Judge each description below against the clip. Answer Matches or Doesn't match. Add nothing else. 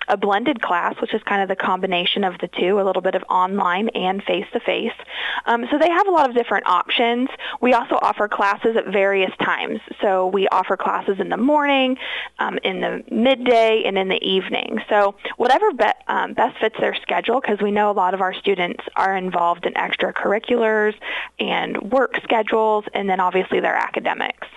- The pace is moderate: Matches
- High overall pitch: Matches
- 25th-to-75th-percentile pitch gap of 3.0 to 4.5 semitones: Matches